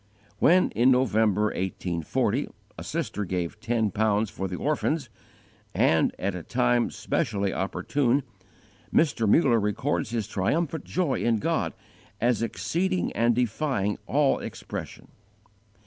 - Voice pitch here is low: Yes, low, 115 Hz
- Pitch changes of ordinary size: Yes, average, 4.9 semitones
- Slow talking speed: Yes, slow, 120 wpm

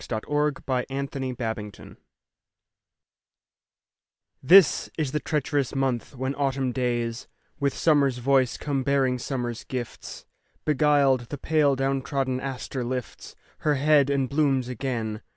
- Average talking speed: No, slow, 120 wpm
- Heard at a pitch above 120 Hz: Yes, low, 135 Hz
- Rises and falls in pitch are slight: Yes, narrow, 2.1 semitones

